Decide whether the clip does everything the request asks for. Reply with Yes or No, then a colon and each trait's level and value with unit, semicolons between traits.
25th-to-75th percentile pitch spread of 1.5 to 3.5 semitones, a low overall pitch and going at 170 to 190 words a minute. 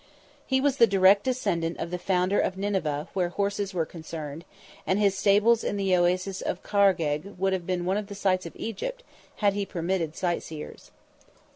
No: narrow, 2.5 semitones; high, 190 Hz; average, 180 wpm